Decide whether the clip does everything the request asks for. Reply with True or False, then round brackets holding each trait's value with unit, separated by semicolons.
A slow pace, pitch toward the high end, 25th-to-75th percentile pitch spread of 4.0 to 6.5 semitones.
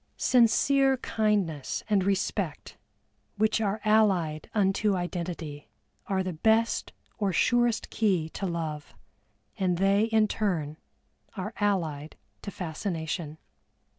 True (105 wpm; 195 Hz; 4.6 semitones)